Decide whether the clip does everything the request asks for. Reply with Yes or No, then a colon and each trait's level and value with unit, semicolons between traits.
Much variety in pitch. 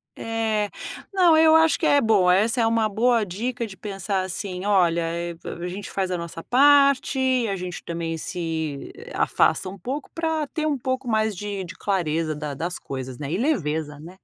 Yes: wide, 6.5 semitones